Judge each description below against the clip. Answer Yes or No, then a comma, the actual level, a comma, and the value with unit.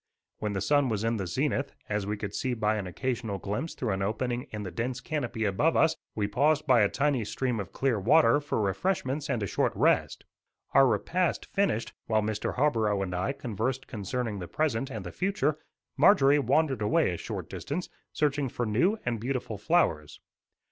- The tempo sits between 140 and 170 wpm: No, average, 190 wpm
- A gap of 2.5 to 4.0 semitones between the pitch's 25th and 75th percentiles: No, wide, 5.4 semitones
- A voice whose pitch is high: No, low, 120 Hz